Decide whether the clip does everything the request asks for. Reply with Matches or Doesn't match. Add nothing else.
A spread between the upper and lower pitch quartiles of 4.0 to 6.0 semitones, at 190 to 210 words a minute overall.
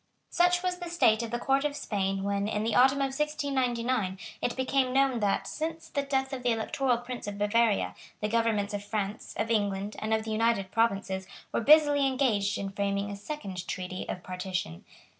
Matches